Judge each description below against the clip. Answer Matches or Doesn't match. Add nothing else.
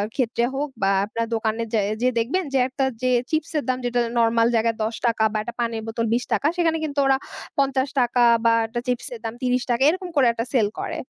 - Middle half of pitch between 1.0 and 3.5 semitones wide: Matches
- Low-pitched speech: Doesn't match